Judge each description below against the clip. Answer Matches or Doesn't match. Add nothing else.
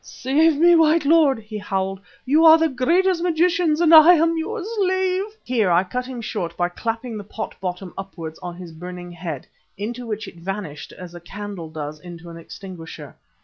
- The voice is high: Matches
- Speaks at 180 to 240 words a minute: Matches